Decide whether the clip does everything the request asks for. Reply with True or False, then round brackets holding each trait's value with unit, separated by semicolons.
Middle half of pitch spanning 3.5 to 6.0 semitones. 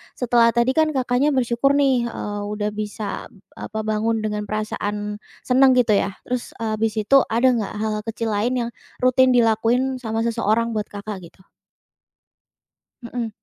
False (2.7 semitones)